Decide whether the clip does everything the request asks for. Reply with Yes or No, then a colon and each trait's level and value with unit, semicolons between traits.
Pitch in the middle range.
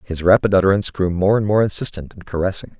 No: very low, 95 Hz